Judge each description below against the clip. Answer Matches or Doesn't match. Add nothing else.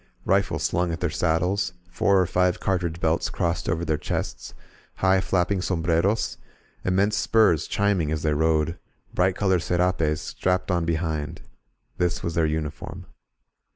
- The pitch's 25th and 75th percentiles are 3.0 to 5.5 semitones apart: Doesn't match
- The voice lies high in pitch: Doesn't match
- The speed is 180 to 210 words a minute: Doesn't match